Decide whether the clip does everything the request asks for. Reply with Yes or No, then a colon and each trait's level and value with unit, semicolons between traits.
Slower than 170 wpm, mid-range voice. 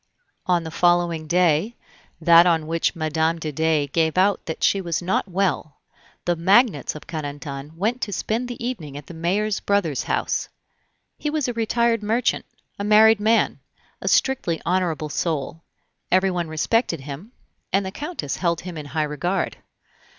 Yes: average, 160 wpm; medium, 175 Hz